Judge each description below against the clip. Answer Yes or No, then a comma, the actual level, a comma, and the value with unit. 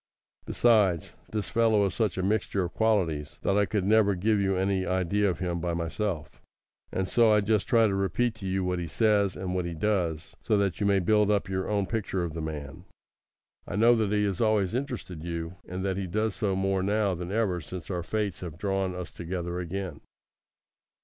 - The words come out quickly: Yes, fast, 210 wpm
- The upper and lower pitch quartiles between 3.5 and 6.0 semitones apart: No, average, 2.9 semitones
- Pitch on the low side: Yes, very low, 95 Hz